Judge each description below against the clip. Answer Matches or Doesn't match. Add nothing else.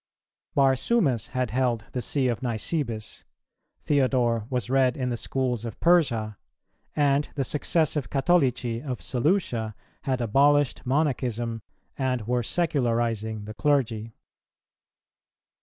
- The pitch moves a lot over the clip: Doesn't match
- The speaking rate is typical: Doesn't match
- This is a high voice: Doesn't match